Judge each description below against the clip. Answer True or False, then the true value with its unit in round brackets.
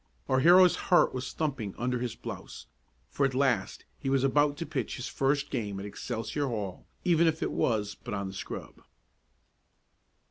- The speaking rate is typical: True (175 wpm)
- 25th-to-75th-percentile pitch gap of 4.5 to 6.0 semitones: True (5.1 semitones)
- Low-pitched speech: True (130 Hz)